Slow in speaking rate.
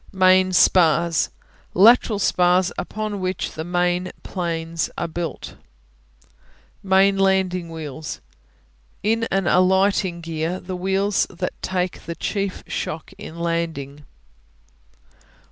Yes: slow, 105 wpm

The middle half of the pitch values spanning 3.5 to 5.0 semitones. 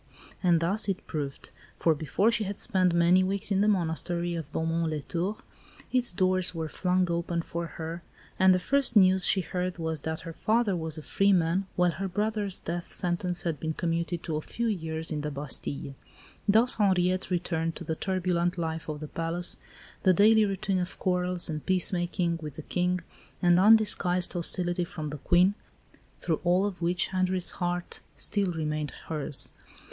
No: narrow, 2.4 semitones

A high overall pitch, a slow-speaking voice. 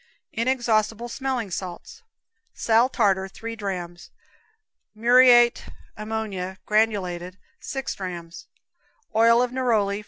Yes: high, 220 Hz; slow, 85 wpm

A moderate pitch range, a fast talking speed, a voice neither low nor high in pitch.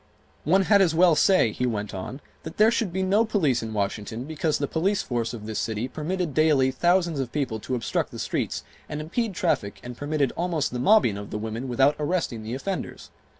No: wide, 7.1 semitones; fast, 210 wpm; medium, 145 Hz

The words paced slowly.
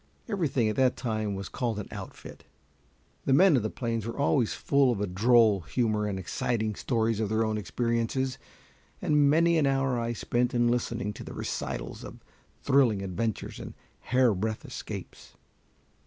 No: average, 165 wpm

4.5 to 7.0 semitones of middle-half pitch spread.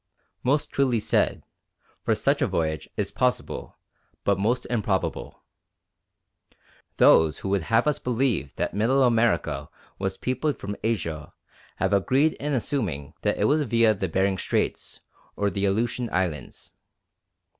Yes: average, 4.8 semitones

